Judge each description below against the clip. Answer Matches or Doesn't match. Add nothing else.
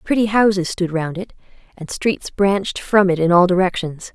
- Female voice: Matches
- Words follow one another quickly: Doesn't match